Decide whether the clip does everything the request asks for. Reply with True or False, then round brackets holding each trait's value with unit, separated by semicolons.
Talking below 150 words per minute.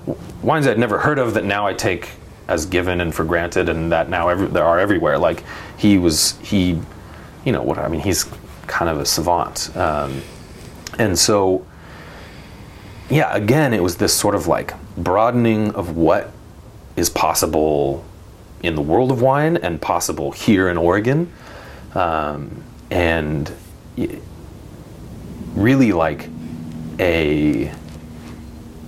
True (140 wpm)